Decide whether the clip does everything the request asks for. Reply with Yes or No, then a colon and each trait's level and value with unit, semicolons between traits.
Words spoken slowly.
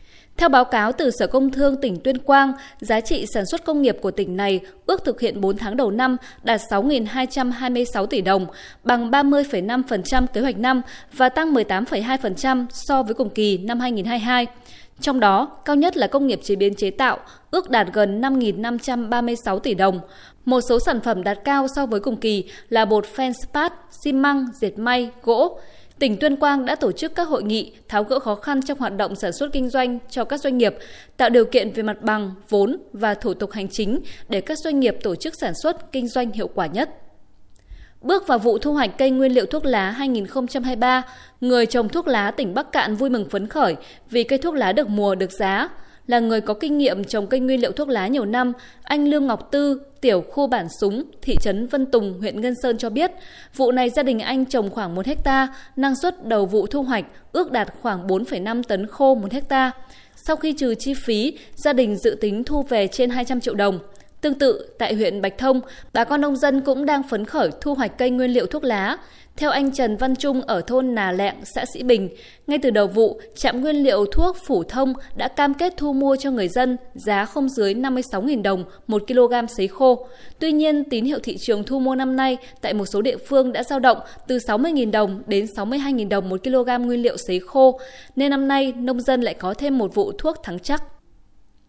No: average, 215 wpm